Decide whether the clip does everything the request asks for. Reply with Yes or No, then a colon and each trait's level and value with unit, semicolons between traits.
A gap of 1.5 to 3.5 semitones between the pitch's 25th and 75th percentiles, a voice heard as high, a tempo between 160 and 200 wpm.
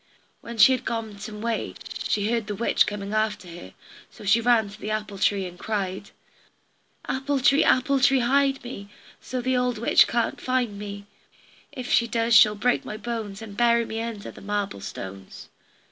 Yes: average, 3.0 semitones; high, 220 Hz; average, 185 wpm